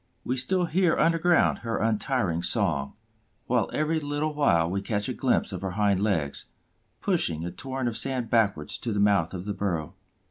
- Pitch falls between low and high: No, low, 110 Hz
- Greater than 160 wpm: Yes, average, 180 wpm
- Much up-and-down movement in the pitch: Yes, wide, 7.3 semitones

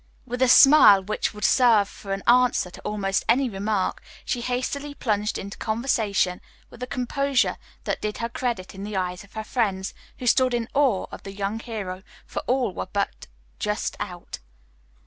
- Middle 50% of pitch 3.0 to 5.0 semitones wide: Yes, average, 4.1 semitones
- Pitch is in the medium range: No, high, 215 Hz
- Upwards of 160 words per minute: Yes, average, 180 wpm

